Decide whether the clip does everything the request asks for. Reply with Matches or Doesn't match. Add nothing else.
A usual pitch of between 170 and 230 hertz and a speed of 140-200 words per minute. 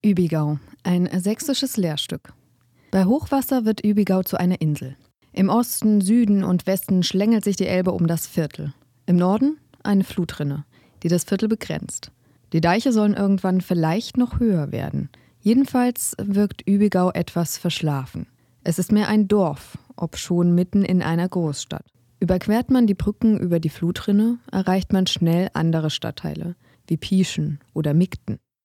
Matches